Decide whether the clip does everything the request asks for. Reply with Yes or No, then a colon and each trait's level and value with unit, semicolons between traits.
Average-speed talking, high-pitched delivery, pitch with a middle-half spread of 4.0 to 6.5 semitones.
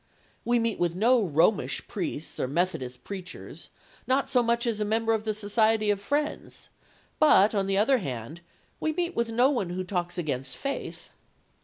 Yes: average, 175 wpm; high, 210 Hz; average, 5.0 semitones